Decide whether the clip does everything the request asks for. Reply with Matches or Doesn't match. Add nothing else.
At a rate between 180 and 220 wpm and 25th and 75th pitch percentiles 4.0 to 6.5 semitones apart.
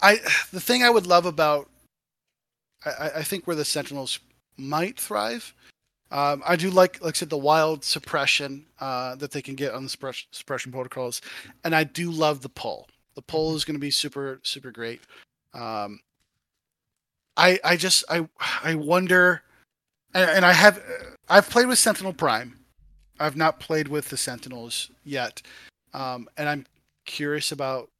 Doesn't match